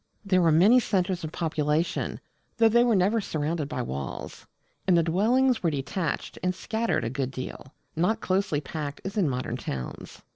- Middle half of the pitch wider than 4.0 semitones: Yes, wide, 5.5 semitones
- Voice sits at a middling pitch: Yes, medium, 170 Hz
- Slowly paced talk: No, average, 175 wpm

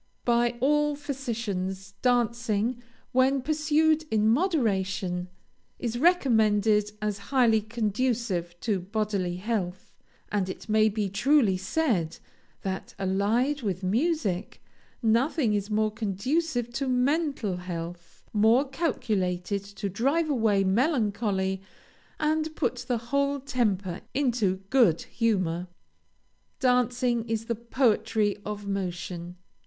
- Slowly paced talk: Yes, slow, 105 wpm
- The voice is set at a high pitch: Yes, high, 220 Hz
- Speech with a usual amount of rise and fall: Yes, average, 4.7 semitones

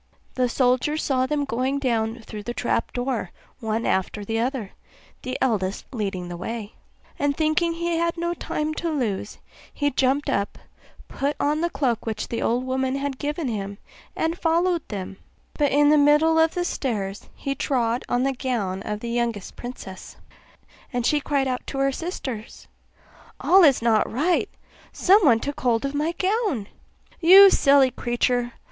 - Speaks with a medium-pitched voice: No, very high, 260 Hz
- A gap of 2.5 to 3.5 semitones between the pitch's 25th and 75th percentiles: No, average, 4.6 semitones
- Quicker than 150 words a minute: Yes, average, 165 wpm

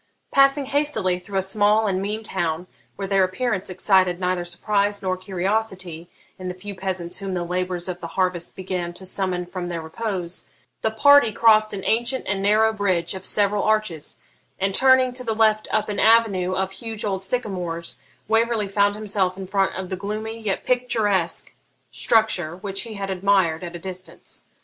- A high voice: Yes, high, 195 Hz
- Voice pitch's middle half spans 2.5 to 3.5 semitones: Yes, average, 2.9 semitones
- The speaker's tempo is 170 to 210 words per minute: Yes, average, 180 wpm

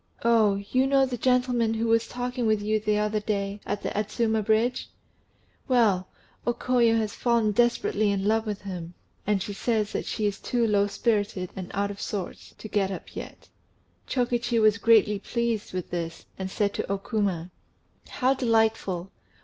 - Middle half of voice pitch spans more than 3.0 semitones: No, average, 2.7 semitones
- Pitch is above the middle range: Yes, high, 215 Hz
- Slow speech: No, average, 180 wpm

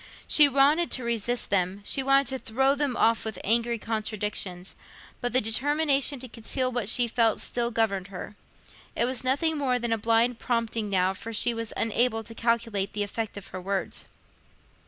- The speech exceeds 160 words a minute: Yes, average, 175 wpm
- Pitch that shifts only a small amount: No, average, 3.3 semitones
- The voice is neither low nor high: No, high, 230 Hz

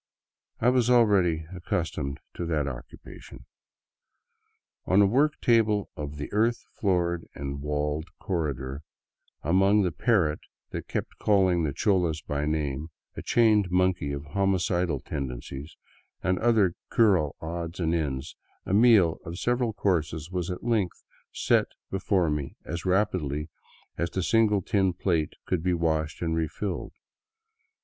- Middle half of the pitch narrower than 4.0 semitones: No, average, 4.6 semitones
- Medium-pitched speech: No, very low, 85 Hz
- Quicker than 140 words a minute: No, slow, 135 wpm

